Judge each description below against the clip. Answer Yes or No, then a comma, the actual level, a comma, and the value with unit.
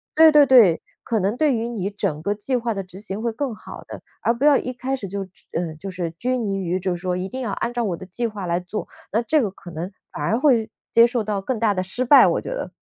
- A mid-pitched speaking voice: No, high, 215 Hz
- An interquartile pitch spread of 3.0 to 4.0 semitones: No, average, 4.7 semitones